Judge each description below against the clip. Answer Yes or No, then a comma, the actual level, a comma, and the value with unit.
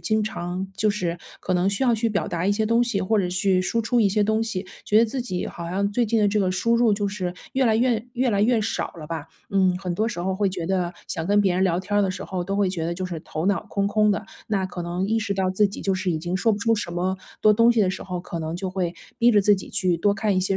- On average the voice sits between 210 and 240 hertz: No, high, 195 Hz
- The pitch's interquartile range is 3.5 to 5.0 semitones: No, average, 2.8 semitones